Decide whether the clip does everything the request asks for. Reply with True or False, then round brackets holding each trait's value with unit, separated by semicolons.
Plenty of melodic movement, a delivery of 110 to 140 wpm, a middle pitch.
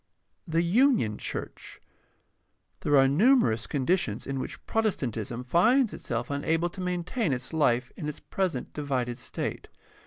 True (6.4 semitones; 135 wpm; 150 Hz)